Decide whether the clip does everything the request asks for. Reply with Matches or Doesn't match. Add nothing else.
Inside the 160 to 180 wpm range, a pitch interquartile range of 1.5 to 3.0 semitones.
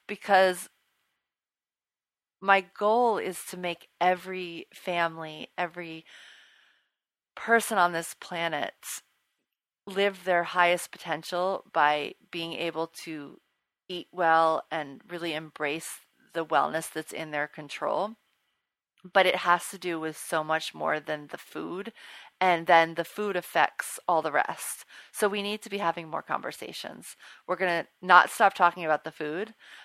Doesn't match